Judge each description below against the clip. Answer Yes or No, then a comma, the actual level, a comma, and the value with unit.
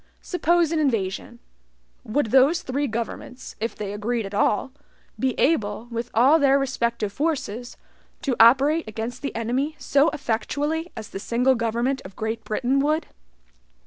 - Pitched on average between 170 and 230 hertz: No, very high, 250 Hz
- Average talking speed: Yes, average, 145 wpm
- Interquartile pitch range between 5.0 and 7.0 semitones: No, average, 4.2 semitones